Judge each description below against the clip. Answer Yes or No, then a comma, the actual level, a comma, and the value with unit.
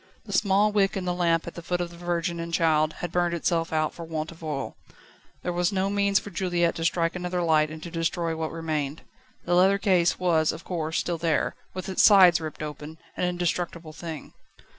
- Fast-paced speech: Yes, fast, 215 wpm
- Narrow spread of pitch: Yes, narrow, 1.8 semitones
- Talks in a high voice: No, medium, 170 Hz